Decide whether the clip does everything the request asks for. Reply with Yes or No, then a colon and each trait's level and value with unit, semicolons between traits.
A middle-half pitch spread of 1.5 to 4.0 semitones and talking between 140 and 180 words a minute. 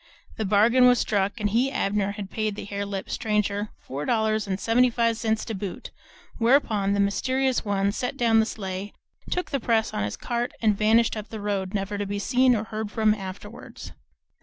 No: narrow, 2.4 semitones; average, 200 wpm